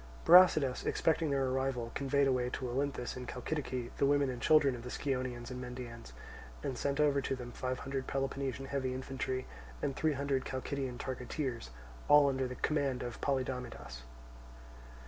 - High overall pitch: No, low, 130 Hz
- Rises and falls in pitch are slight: Yes, narrow, 1.8 semitones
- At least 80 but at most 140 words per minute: No, average, 160 wpm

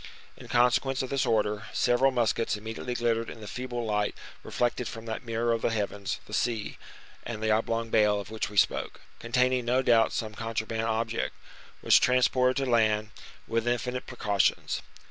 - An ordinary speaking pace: Yes, average, 170 wpm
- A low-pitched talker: Yes, low, 115 Hz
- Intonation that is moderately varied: No, narrow, 2.0 semitones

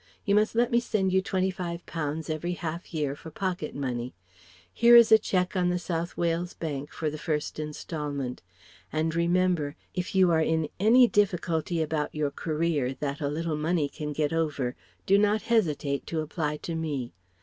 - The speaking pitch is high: No, medium, 165 Hz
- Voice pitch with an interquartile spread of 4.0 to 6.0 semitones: No, average, 3.5 semitones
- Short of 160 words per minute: No, average, 185 wpm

